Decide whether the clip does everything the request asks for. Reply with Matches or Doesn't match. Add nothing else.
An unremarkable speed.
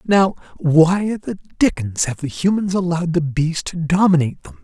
Matches